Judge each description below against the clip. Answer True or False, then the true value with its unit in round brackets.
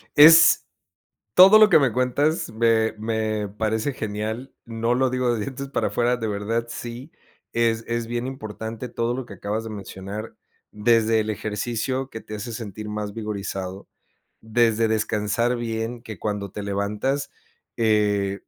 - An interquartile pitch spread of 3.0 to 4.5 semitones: False (2.4 semitones)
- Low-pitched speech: True (110 Hz)